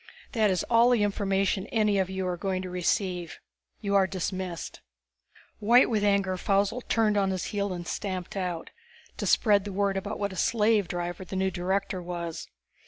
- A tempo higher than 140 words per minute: Yes, average, 180 wpm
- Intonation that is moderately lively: No, narrow, 2.0 semitones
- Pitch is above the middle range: Yes, high, 195 Hz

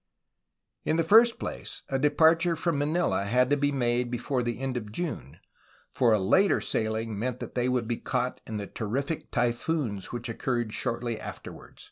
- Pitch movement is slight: No, average, 4.2 semitones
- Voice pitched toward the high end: No, low, 125 Hz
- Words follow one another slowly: No, average, 175 wpm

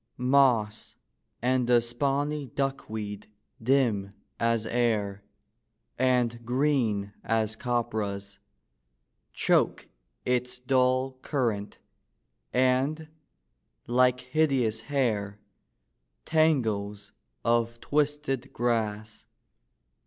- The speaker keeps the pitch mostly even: No, average, 3.5 semitones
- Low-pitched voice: Yes, low, 120 Hz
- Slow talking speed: Yes, slow, 70 wpm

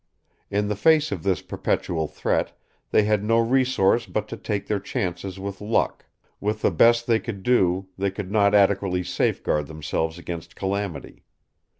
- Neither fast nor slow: Yes, average, 165 wpm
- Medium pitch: No, low, 100 Hz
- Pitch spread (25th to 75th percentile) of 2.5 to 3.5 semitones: Yes, average, 2.8 semitones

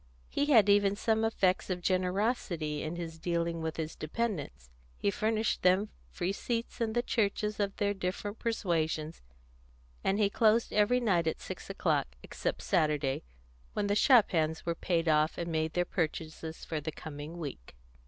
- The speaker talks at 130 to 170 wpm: Yes, average, 165 wpm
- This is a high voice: No, medium, 180 Hz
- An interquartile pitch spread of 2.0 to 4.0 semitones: No, average, 4.7 semitones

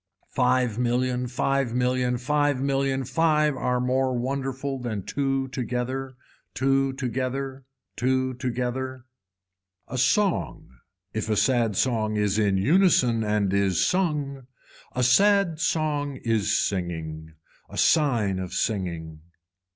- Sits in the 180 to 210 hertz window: No, low, 130 Hz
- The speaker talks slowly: Yes, slow, 115 wpm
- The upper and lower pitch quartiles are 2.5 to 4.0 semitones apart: Yes, average, 3.2 semitones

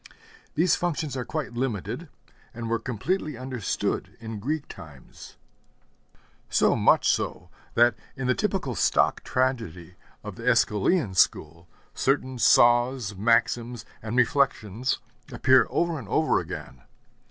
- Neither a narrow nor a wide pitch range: Yes, average, 3.8 semitones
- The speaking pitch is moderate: No, low, 120 Hz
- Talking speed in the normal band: No, slow, 120 wpm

